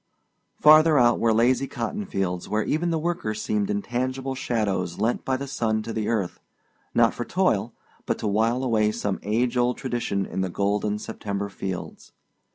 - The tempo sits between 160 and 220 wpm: Yes, average, 170 wpm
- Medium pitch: No, low, 110 Hz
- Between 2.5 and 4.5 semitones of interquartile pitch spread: Yes, average, 4.0 semitones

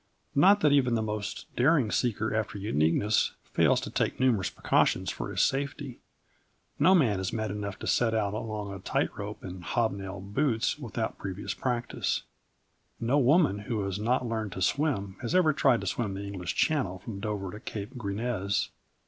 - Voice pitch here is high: No, low, 110 Hz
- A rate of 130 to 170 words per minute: No, average, 180 wpm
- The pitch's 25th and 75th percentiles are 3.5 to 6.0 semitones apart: Yes, average, 4.2 semitones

